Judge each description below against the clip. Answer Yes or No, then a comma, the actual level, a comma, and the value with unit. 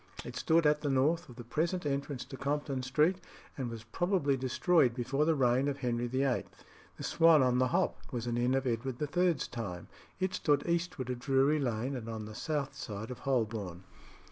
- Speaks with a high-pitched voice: No, low, 135 Hz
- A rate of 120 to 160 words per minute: No, average, 195 wpm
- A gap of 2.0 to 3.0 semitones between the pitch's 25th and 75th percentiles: No, average, 3.8 semitones